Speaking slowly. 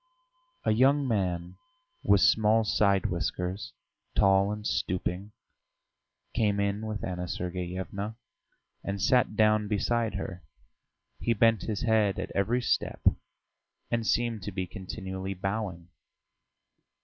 Yes: slow, 115 wpm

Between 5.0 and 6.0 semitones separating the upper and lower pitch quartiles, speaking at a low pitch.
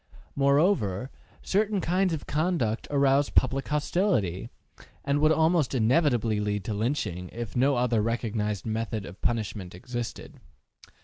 Yes: wide, 5.6 semitones; low, 125 Hz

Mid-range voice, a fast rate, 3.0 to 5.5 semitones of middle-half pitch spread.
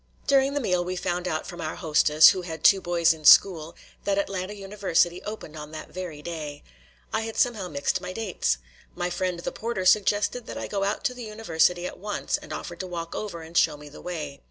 Yes: medium, 180 Hz; fast, 220 wpm; average, 3.7 semitones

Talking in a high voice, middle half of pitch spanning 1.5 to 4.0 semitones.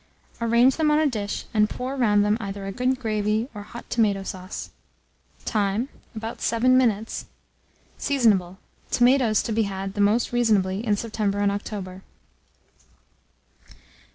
Yes: high, 215 Hz; average, 3.0 semitones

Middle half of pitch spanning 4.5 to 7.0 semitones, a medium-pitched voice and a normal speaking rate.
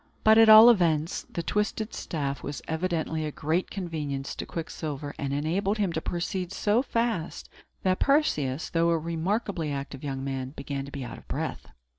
Yes: wide, 5.4 semitones; medium, 165 Hz; average, 175 wpm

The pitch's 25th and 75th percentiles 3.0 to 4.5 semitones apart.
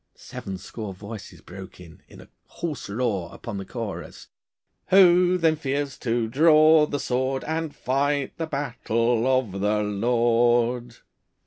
No: average, 5.2 semitones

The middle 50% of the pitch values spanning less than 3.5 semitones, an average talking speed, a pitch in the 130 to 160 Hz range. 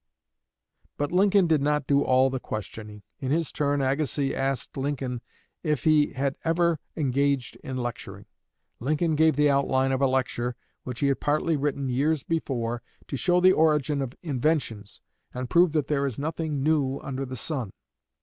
Yes: average, 2.9 semitones; average, 170 wpm; medium, 140 Hz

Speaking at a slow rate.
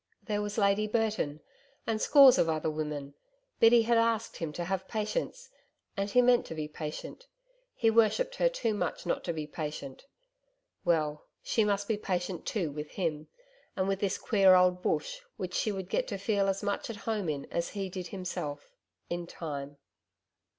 No: average, 180 wpm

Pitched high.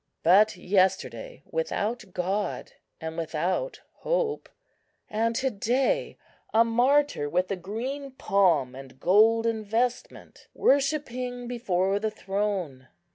Yes: high, 220 Hz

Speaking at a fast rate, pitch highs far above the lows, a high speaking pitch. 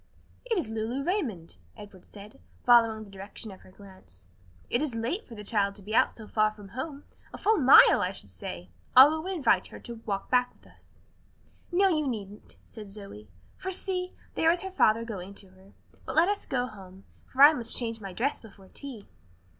Yes: fast, 210 wpm; wide, 6.1 semitones; high, 225 Hz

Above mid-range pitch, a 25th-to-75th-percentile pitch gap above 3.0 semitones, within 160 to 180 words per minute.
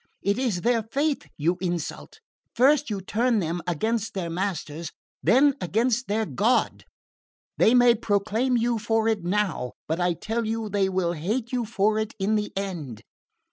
Yes: high, 215 Hz; average, 4.4 semitones; average, 165 wpm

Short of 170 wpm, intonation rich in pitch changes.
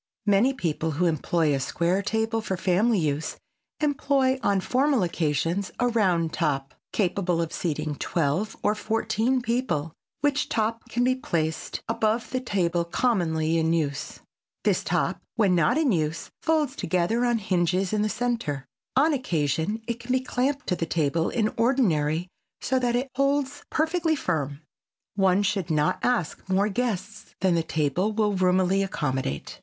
Yes: average, 155 wpm; wide, 6.8 semitones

